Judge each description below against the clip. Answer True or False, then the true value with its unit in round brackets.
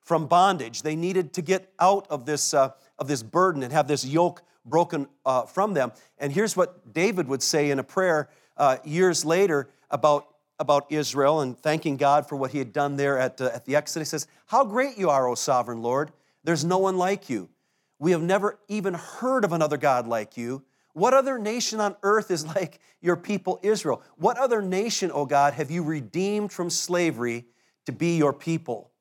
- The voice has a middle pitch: True (155 Hz)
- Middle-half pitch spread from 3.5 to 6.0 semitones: True (4.6 semitones)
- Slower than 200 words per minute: False (205 wpm)